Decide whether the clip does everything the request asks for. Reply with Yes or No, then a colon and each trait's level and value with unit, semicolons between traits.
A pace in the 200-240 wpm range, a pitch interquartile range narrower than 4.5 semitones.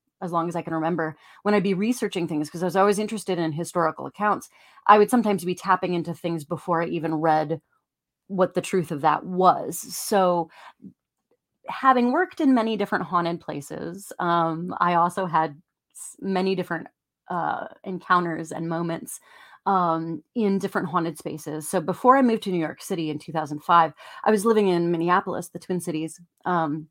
No: average, 175 wpm; average, 3.1 semitones